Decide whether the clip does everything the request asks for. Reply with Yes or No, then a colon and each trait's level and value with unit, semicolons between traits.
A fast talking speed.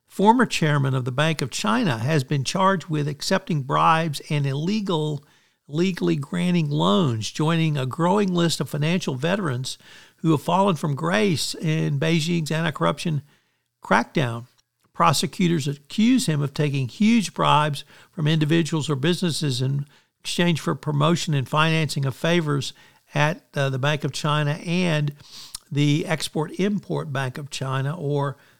No: average, 140 wpm